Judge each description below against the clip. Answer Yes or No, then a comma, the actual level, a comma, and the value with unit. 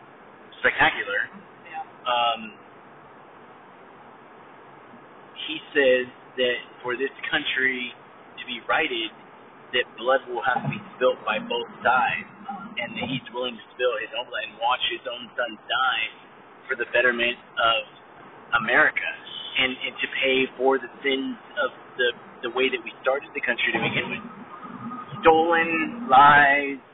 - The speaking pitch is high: No, low, 135 Hz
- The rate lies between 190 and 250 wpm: No, slow, 135 wpm